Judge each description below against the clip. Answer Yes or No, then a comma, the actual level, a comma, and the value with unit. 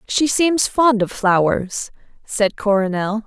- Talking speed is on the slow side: Yes, slow, 130 wpm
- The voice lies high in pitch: Yes, high, 220 Hz